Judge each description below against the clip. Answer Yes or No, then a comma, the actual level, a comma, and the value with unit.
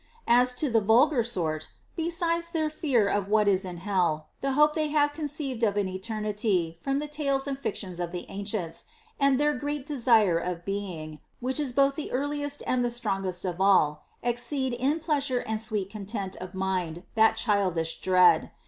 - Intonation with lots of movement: Yes, wide, 6.8 semitones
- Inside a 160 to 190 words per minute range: Yes, average, 185 wpm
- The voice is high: Yes, high, 225 Hz